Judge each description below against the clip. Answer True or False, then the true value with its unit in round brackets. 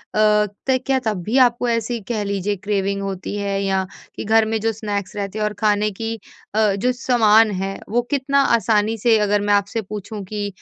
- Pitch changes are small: True (1.9 semitones)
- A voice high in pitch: True (210 Hz)